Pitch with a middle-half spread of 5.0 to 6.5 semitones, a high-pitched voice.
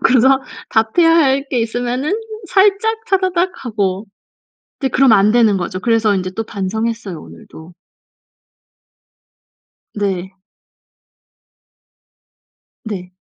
Yes: wide, 5.6 semitones; high, 225 Hz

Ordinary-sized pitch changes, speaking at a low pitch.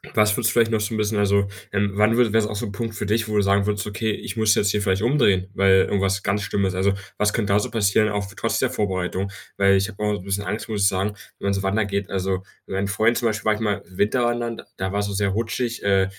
No: narrow, 1.8 semitones; low, 100 Hz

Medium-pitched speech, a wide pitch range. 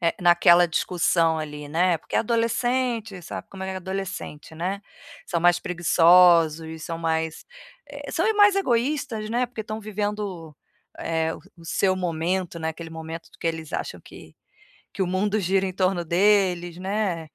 No: medium, 180 Hz; average, 3.8 semitones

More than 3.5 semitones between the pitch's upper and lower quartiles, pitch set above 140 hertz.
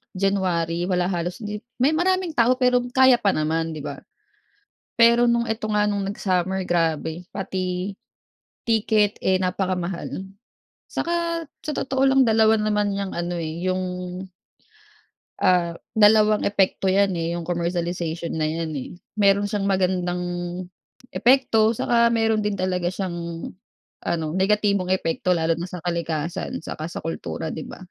Yes: average, 3.9 semitones; high, 190 Hz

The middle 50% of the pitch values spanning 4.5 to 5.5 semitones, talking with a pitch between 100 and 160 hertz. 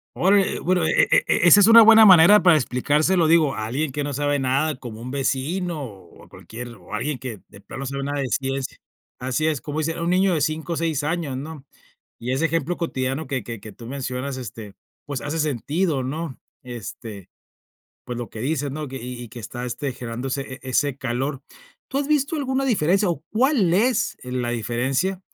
Yes: average, 4.8 semitones; medium, 140 Hz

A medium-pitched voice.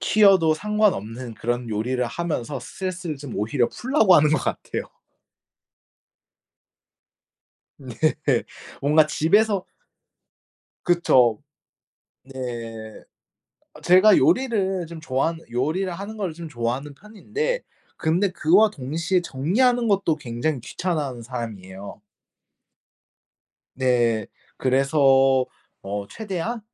Yes: medium, 155 Hz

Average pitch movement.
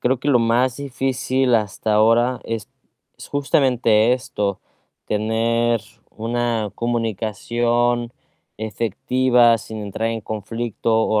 No: narrow, 1.9 semitones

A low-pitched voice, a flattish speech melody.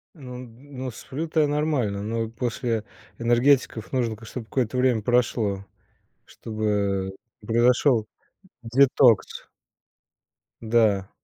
No: low, 120 Hz; average, 3.0 semitones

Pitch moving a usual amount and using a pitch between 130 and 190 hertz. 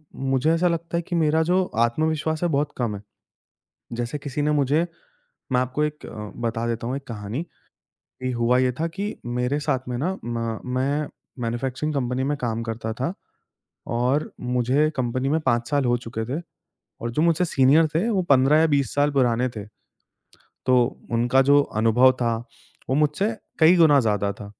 Yes: average, 4.1 semitones; low, 135 Hz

